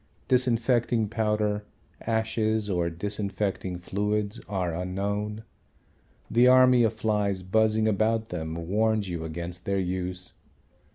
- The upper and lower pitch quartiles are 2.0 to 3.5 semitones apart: Yes, average, 3.2 semitones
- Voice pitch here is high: No, low, 105 Hz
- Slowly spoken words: Yes, slow, 110 wpm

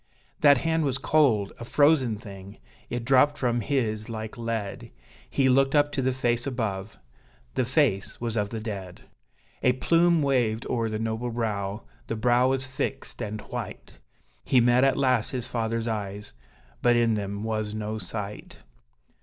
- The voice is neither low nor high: No, low, 115 Hz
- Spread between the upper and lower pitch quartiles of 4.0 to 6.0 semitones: No, average, 3.5 semitones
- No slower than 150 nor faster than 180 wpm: Yes, average, 160 wpm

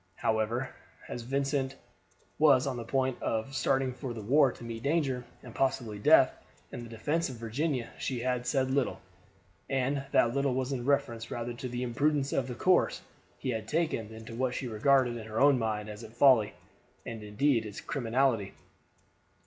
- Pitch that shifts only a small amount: No, average, 3.0 semitones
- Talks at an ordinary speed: Yes, average, 180 wpm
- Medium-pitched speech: No, low, 125 Hz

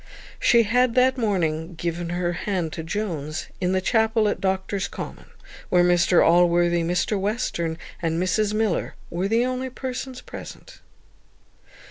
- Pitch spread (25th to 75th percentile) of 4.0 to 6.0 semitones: Yes, average, 4.5 semitones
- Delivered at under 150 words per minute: Yes, average, 140 wpm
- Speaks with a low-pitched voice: No, high, 190 Hz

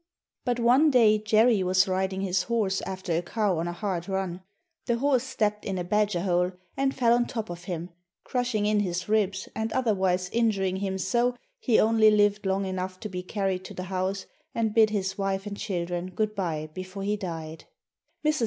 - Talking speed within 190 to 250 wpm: Yes, average, 195 wpm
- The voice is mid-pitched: No, high, 195 Hz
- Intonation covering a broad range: No, average, 3.1 semitones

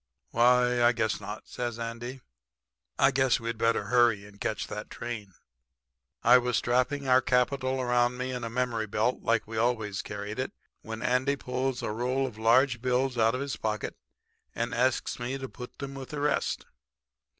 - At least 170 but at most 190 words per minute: Yes, average, 180 wpm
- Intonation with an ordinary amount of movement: No, narrow, 2.2 semitones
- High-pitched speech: No, low, 120 Hz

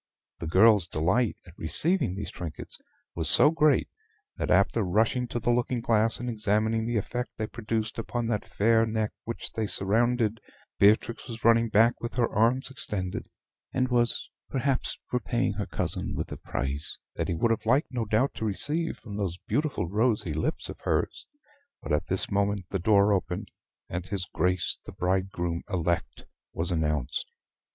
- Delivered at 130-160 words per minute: No, average, 170 wpm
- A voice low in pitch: Yes, low, 110 Hz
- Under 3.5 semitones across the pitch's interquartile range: No, average, 4.2 semitones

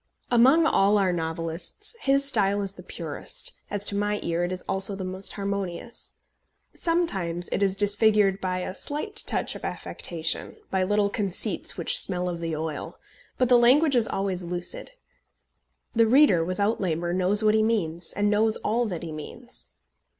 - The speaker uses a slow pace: No, average, 170 wpm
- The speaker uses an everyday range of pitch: Yes, average, 4.3 semitones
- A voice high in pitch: Yes, high, 200 Hz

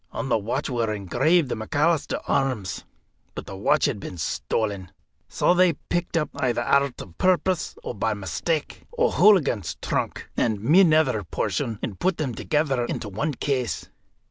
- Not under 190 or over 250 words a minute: No, average, 160 wpm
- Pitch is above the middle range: No, low, 130 Hz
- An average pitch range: No, wide, 6.7 semitones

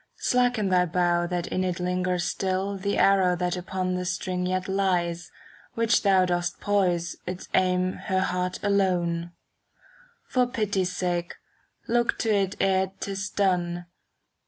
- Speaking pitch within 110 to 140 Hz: No, medium, 185 Hz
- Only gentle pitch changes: Yes, narrow, 1.7 semitones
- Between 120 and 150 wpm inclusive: Yes, average, 145 wpm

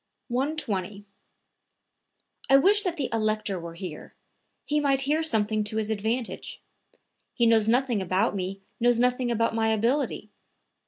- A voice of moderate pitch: No, high, 225 Hz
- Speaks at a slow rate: No, average, 145 wpm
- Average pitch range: Yes, average, 4.2 semitones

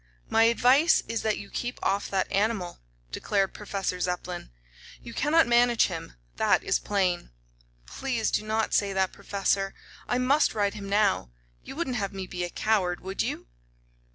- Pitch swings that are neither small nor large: Yes, average, 3.4 semitones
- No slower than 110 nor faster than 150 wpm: No, average, 165 wpm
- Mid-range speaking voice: No, high, 205 Hz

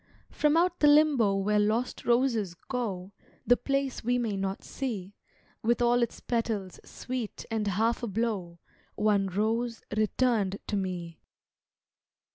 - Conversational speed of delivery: No, slow, 130 wpm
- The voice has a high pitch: Yes, high, 225 Hz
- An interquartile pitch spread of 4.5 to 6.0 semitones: No, average, 3.7 semitones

